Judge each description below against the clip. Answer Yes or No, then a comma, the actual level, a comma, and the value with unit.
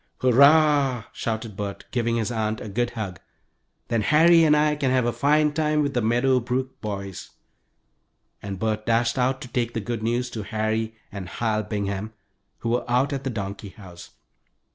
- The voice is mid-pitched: No, low, 115 Hz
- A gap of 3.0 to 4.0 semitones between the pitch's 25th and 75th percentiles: Yes, average, 3.5 semitones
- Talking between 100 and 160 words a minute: No, average, 180 wpm